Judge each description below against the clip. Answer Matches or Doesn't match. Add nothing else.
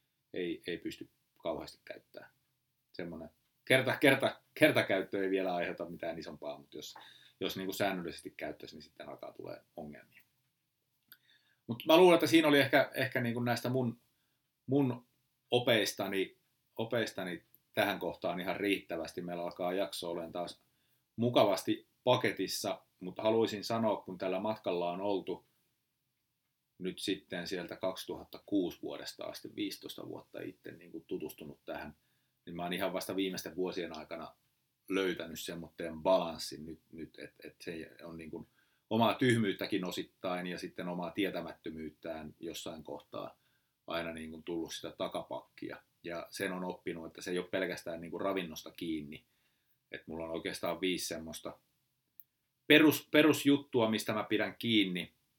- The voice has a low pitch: Matches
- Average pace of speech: Matches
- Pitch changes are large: Matches